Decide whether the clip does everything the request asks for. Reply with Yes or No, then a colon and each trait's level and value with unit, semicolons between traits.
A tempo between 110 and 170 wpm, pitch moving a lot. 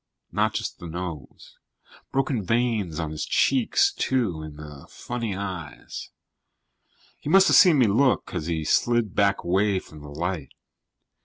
Yes: average, 150 wpm; wide, 7.3 semitones